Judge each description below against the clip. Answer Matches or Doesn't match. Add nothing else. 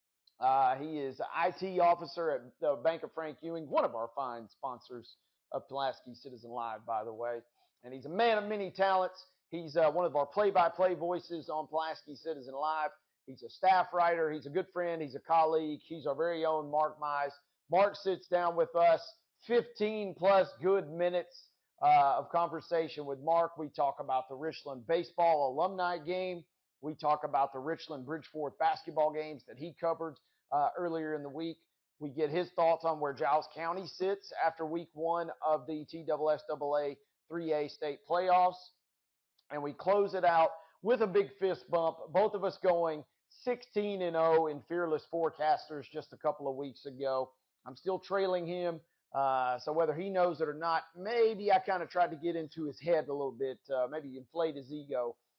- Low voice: Doesn't match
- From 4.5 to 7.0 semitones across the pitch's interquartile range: Doesn't match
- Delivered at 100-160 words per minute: Doesn't match